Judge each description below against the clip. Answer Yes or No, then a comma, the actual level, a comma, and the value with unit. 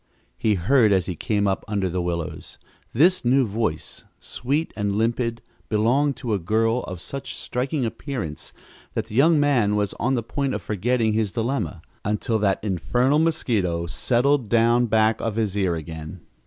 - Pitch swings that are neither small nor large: Yes, average, 4.3 semitones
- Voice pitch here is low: Yes, low, 110 Hz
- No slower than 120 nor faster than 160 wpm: No, average, 170 wpm